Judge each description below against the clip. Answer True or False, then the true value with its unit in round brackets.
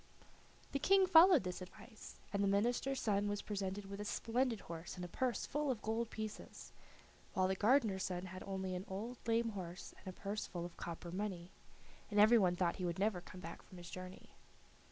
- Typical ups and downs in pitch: True (3.8 semitones)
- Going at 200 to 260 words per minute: True (205 wpm)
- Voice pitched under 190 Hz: False (200 Hz)